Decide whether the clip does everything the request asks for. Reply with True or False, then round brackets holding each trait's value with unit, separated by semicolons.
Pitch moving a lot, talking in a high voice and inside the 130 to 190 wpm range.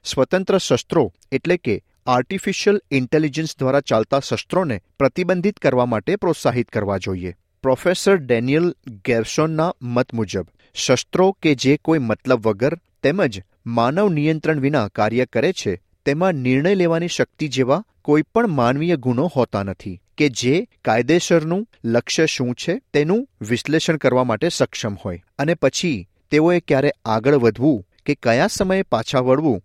False (6.2 semitones; 135 Hz; 135 wpm)